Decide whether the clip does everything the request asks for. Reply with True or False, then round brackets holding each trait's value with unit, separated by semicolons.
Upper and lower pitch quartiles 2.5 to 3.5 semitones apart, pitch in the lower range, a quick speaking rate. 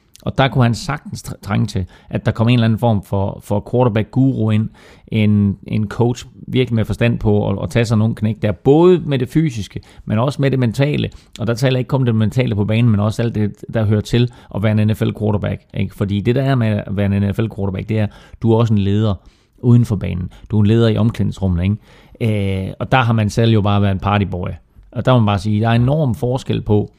True (2.8 semitones; 110 Hz; 250 wpm)